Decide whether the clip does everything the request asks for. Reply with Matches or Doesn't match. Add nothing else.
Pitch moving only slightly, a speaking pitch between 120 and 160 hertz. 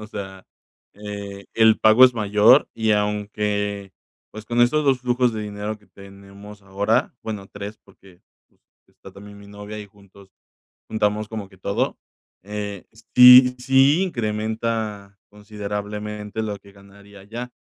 Doesn't match